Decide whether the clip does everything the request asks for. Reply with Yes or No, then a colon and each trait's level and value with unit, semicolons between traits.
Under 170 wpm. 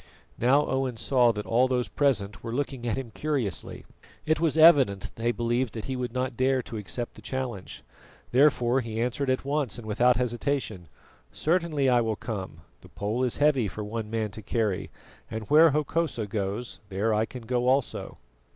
No: average, 180 wpm